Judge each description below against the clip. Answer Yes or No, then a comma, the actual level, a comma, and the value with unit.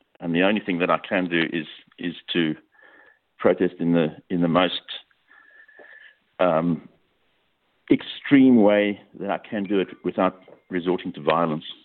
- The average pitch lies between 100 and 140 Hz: No, very low, 90 Hz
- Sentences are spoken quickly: No, average, 145 wpm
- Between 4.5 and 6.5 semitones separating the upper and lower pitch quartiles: No, average, 3.8 semitones